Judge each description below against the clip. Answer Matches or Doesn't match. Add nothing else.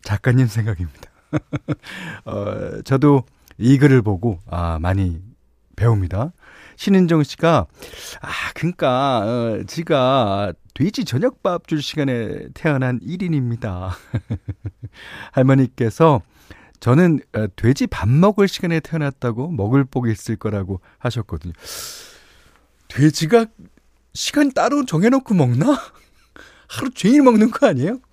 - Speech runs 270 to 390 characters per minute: Doesn't match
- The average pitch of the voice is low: Matches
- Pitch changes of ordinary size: Doesn't match